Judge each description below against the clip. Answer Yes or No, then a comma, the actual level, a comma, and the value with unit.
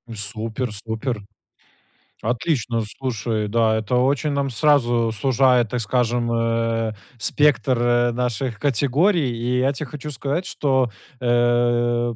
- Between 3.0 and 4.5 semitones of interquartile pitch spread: No, narrow, 2.6 semitones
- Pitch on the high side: No, low, 120 Hz